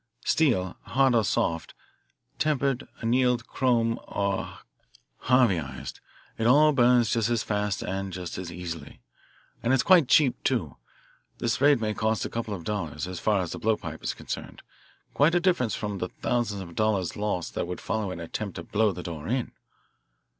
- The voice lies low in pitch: Yes, low, 110 Hz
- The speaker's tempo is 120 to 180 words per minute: Yes, average, 170 wpm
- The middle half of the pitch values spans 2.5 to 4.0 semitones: No, average, 5.1 semitones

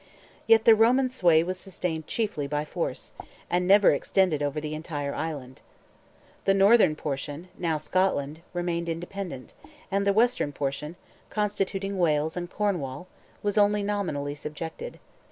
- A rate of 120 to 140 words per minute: Yes, slow, 135 wpm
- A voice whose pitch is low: No, medium, 175 Hz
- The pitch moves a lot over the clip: No, average, 4.9 semitones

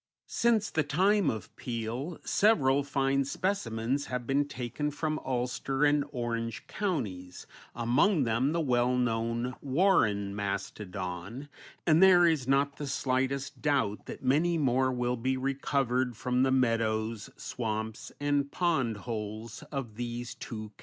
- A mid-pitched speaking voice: No, low, 130 Hz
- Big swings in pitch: No, average, 3.9 semitones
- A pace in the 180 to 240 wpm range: No, slow, 135 wpm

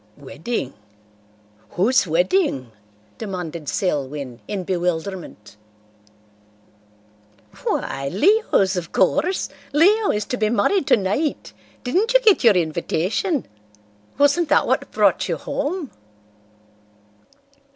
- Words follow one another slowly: Yes, slow, 95 wpm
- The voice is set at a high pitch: Yes, high, 200 Hz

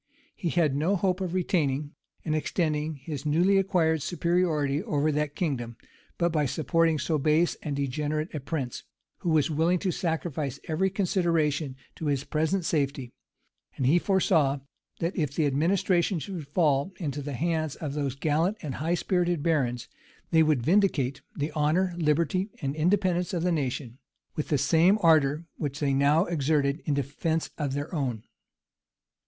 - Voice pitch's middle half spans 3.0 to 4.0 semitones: Yes, average, 3.4 semitones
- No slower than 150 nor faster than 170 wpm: Yes, average, 160 wpm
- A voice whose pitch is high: No, medium, 155 Hz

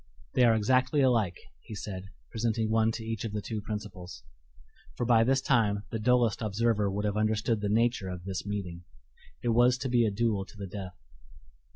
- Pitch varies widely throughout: No, narrow, 2.6 semitones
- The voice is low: Yes, low, 110 Hz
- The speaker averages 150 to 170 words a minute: No, average, 195 wpm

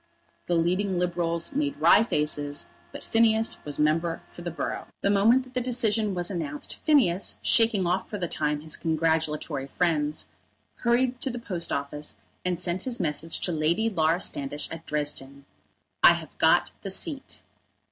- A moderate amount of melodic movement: No, wide, 6.2 semitones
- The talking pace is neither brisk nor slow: Yes, average, 165 wpm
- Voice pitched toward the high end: No, medium, 175 Hz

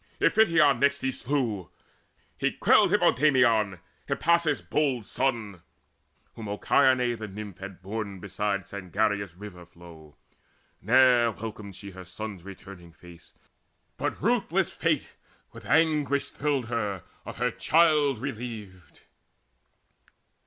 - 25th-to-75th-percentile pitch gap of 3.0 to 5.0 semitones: No, wide, 5.6 semitones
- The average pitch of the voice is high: No, low, 110 Hz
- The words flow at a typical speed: No, slow, 110 wpm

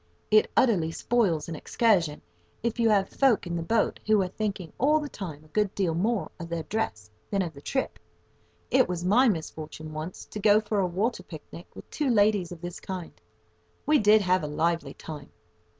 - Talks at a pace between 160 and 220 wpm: Yes, average, 200 wpm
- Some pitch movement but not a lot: Yes, average, 4.8 semitones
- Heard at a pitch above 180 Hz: Yes, high, 190 Hz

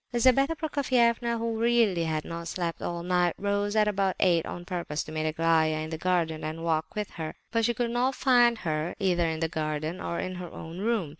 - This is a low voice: No, medium, 180 Hz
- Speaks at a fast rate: Yes, fast, 215 wpm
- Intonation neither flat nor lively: No, wide, 6.0 semitones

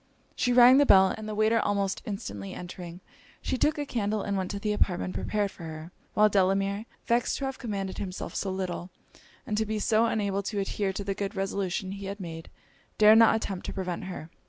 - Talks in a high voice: Yes, high, 200 Hz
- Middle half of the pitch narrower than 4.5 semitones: Yes, narrow, 2.4 semitones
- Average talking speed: No, fast, 210 wpm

